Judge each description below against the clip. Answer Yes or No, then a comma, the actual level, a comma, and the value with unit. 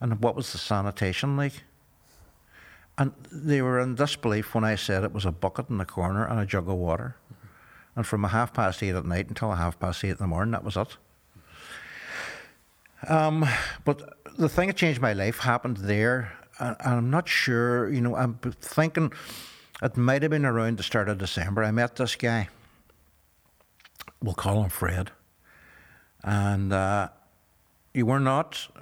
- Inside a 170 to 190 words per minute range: Yes, average, 175 wpm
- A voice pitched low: Yes, low, 115 Hz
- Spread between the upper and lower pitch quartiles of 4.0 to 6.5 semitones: Yes, average, 4.7 semitones